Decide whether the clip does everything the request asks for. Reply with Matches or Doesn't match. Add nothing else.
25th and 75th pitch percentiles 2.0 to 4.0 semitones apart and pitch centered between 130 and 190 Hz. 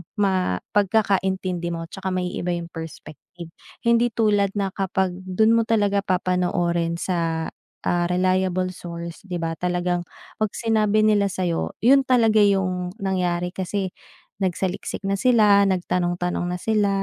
Matches